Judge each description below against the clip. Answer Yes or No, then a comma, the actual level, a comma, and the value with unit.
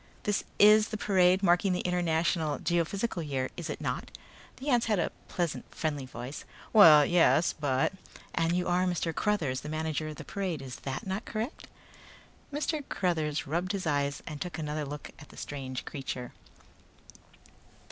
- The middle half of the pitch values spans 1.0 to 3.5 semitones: No, average, 4.3 semitones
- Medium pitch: Yes, medium, 165 Hz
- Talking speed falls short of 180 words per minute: Yes, average, 165 wpm